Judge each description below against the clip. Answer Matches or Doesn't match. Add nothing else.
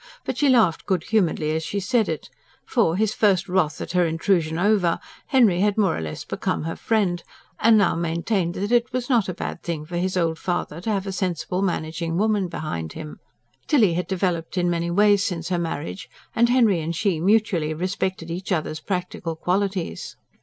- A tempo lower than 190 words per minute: Doesn't match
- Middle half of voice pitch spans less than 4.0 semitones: Matches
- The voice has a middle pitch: Matches